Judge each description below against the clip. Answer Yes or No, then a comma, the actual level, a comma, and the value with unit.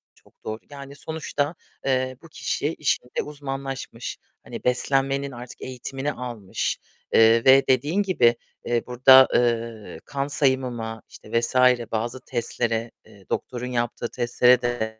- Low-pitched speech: Yes, low, 125 Hz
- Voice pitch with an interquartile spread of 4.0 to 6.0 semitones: No, average, 2.7 semitones